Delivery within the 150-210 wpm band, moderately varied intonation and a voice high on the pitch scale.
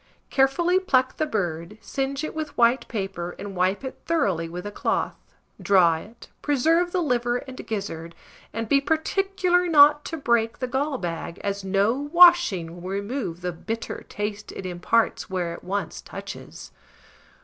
No: average, 160 wpm; wide, 7.5 semitones; high, 230 Hz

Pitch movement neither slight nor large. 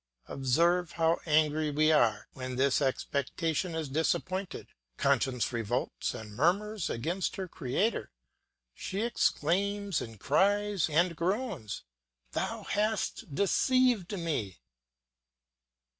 No: wide, 6.3 semitones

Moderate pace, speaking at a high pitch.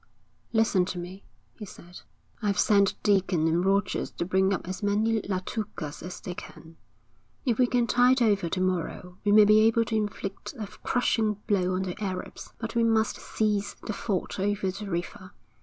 Yes: average, 180 wpm; high, 200 Hz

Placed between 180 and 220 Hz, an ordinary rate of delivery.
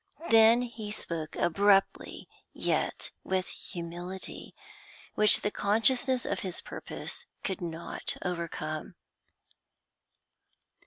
No: high, 190 Hz; slow, 90 wpm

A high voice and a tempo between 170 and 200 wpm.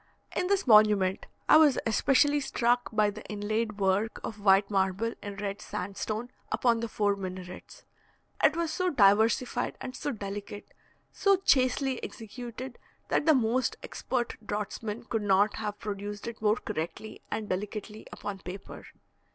No: high, 215 Hz; average, 145 wpm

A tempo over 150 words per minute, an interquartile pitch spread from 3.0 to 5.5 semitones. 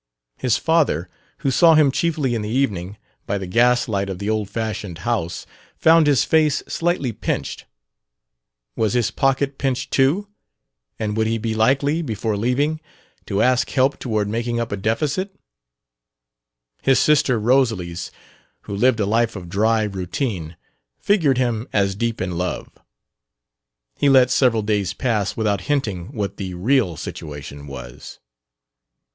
No: average, 145 wpm; average, 5.1 semitones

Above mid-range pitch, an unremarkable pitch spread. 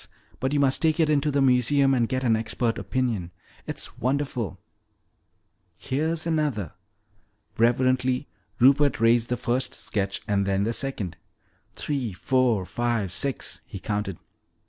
No: low, 125 Hz; average, 3.9 semitones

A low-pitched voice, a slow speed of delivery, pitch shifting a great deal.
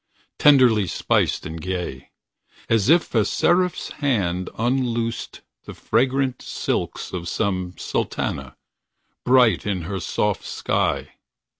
Yes: low, 110 Hz; slow, 110 wpm; wide, 5.9 semitones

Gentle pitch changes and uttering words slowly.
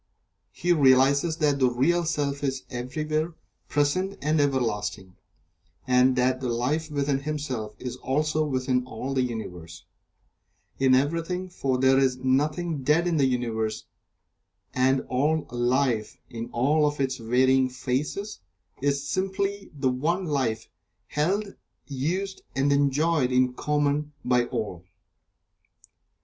No: average, 3.3 semitones; slow, 125 wpm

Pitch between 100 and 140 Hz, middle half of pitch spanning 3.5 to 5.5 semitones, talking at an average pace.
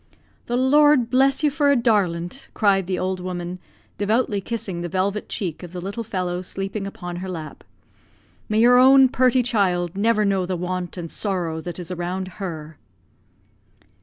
No: high, 195 Hz; average, 4.5 semitones; average, 165 wpm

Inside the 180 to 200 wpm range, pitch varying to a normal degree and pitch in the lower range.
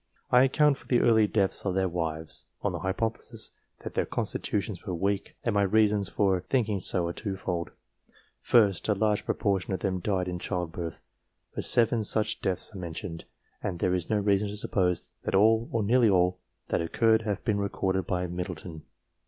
Yes: average, 190 wpm; average, 3.1 semitones; low, 100 Hz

